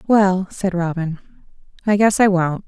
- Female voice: Yes, female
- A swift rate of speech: No, average, 155 wpm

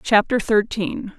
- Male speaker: No, female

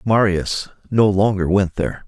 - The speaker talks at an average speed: Yes, average, 145 wpm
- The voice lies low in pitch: Yes, low, 100 Hz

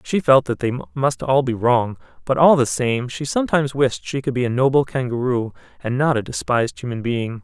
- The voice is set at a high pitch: No, low, 125 Hz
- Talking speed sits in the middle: No, fast, 220 wpm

